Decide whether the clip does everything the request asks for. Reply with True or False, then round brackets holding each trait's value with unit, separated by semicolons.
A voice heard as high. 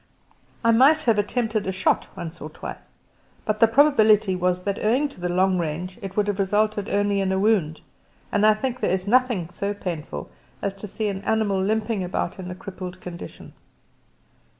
True (200 Hz)